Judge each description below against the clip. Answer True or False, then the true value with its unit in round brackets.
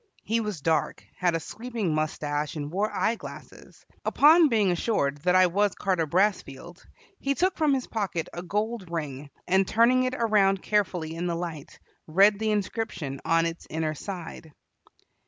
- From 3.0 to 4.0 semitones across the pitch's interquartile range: False (5.0 semitones)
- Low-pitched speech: False (185 Hz)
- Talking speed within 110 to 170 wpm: True (165 wpm)